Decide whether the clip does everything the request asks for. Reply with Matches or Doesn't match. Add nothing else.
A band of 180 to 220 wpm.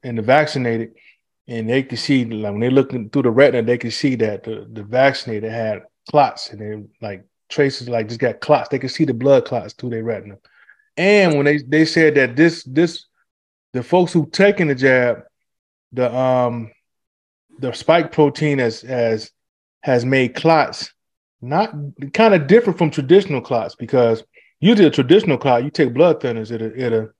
Matches